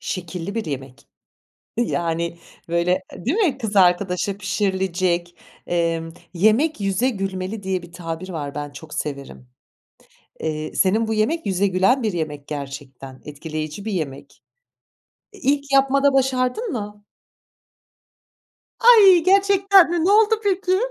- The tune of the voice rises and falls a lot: Yes, wide, 8.2 semitones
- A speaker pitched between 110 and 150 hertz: No, high, 190 Hz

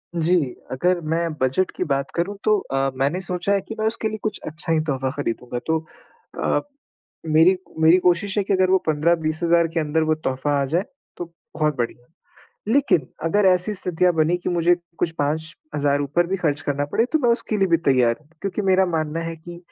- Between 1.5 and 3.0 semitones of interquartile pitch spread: No, average, 3.7 semitones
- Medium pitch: Yes, medium, 165 Hz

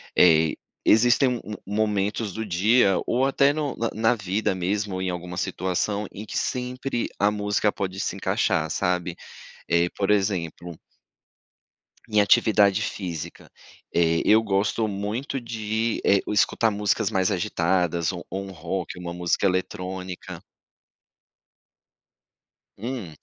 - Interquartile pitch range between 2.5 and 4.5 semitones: Yes, average, 3.3 semitones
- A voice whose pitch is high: No, low, 100 Hz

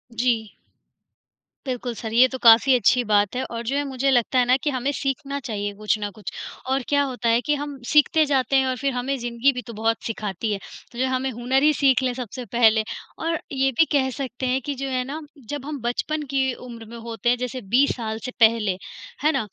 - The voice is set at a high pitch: Yes, very high, 250 Hz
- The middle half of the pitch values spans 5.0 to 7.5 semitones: No, average, 2.9 semitones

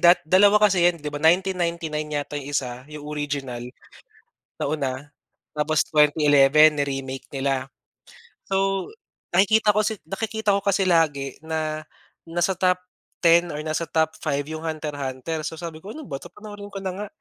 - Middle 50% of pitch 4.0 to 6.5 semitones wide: Yes, average, 4.3 semitones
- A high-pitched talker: No, medium, 160 Hz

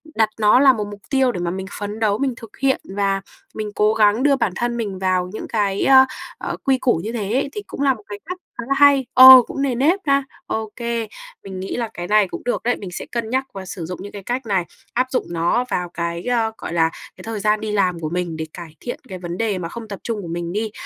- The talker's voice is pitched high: Yes, high, 215 Hz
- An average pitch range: Yes, average, 4.7 semitones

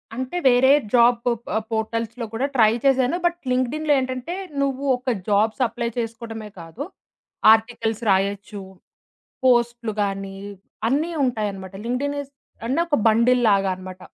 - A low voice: No, high, 235 Hz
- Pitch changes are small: No, average, 3.2 semitones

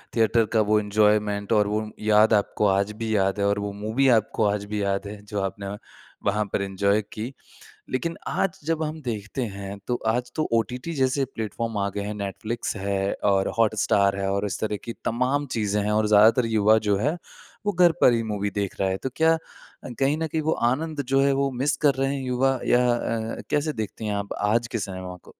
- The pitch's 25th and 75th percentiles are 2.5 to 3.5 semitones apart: No, average, 4.0 semitones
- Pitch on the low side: Yes, low, 110 Hz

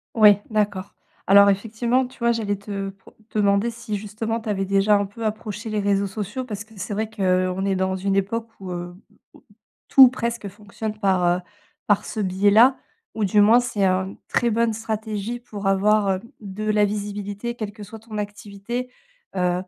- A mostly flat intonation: Yes, narrow, 2.0 semitones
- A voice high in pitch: Yes, high, 205 Hz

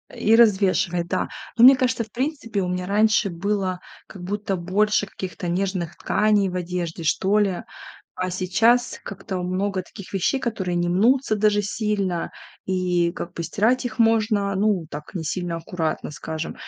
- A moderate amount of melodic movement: Yes, average, 3.1 semitones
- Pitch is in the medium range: No, high, 195 Hz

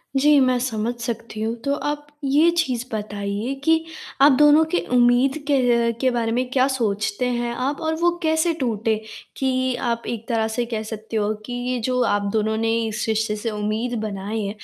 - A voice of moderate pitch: No, high, 240 Hz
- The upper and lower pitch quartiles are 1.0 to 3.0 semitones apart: No, average, 3.4 semitones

